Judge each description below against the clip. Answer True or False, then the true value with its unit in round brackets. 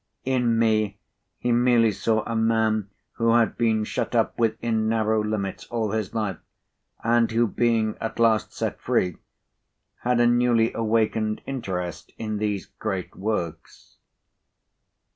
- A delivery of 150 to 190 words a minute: False (135 wpm)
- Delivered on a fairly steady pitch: True (1.4 semitones)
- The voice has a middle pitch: False (110 Hz)